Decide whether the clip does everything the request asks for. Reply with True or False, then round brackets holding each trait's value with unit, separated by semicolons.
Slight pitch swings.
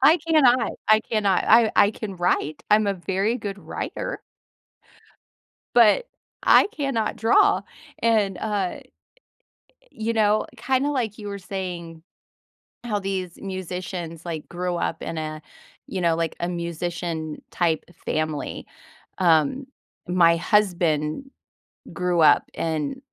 False (4.6 semitones)